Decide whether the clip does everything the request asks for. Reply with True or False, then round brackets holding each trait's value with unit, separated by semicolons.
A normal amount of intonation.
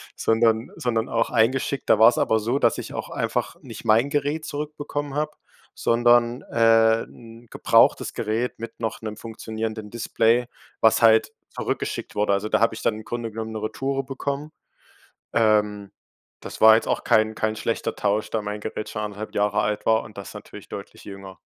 False (1.8 semitones)